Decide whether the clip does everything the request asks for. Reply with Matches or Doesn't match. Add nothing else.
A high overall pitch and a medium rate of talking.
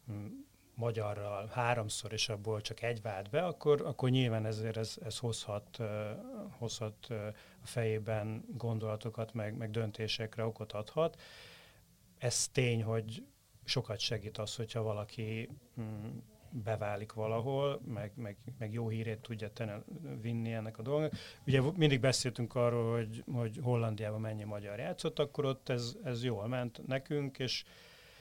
Doesn't match